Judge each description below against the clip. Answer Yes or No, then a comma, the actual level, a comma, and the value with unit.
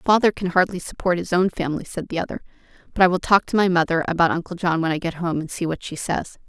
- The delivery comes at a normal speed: No, fast, 270 wpm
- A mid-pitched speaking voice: Yes, medium, 175 Hz